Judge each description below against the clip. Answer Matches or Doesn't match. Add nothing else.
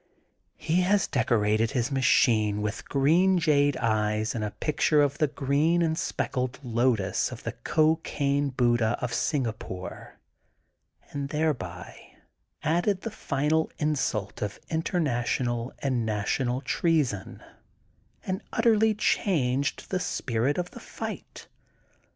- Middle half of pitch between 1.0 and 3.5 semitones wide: Doesn't match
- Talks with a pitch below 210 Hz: Matches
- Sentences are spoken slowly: Matches